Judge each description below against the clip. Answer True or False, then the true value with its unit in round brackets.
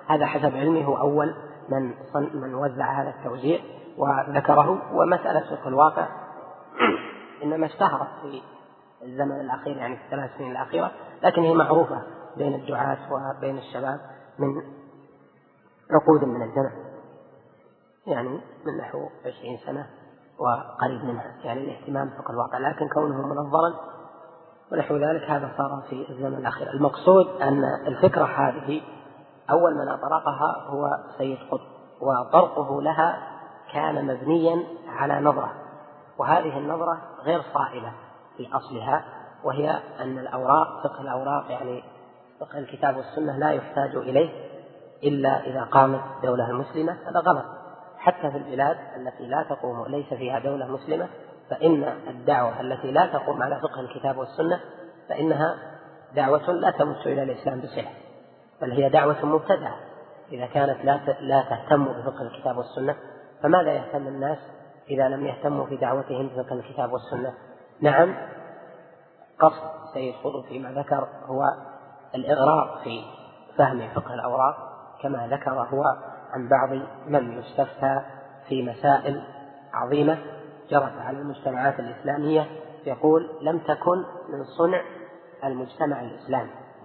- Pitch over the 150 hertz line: False (140 Hz)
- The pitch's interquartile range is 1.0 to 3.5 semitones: True (2.5 semitones)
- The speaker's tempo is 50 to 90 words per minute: False (125 wpm)